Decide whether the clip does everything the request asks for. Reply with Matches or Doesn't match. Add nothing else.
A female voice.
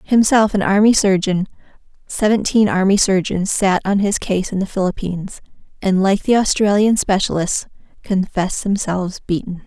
Matches